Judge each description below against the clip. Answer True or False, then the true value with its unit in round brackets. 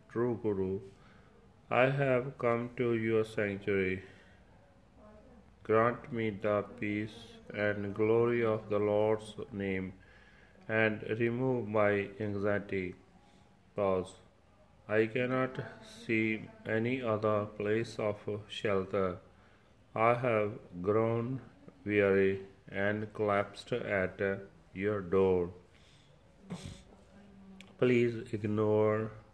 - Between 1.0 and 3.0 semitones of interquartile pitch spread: True (2.5 semitones)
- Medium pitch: False (105 Hz)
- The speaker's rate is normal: False (85 wpm)